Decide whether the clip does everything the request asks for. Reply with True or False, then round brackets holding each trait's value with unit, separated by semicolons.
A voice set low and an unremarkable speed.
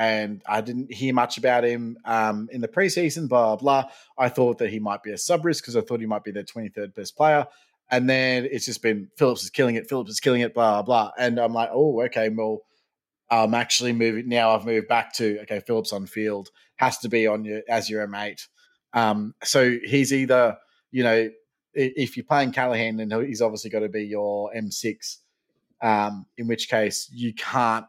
False (115 Hz; 220 wpm)